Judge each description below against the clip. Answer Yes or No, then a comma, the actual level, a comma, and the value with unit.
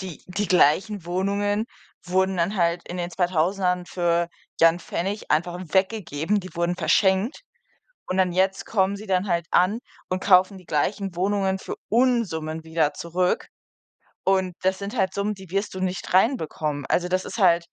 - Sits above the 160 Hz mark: Yes, medium, 185 Hz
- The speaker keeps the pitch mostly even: Yes, narrow, 2.3 semitones